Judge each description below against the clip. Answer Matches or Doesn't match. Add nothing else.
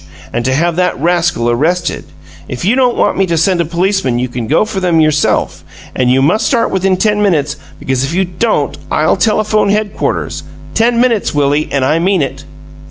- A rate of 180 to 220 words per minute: Matches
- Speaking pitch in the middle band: Matches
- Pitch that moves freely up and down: Matches